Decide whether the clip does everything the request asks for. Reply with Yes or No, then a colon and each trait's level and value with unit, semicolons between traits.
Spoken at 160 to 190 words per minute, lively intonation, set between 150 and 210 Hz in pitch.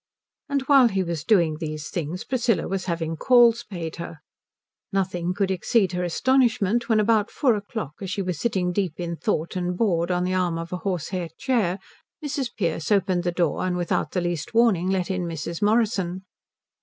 No: average, 185 wpm; average, 3.9 semitones; medium, 185 Hz